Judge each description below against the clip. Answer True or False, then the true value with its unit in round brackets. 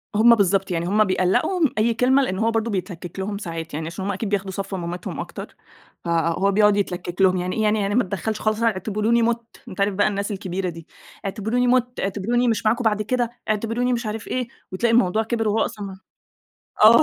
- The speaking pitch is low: False (210 Hz)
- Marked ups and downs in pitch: False (3.3 semitones)